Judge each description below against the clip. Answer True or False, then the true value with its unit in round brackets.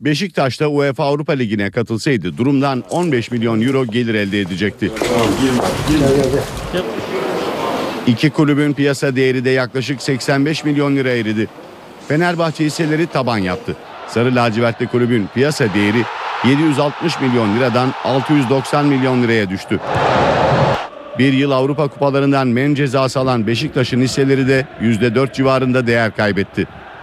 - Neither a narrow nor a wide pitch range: True (3.3 semitones)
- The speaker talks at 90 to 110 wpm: False (120 wpm)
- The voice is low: True (130 Hz)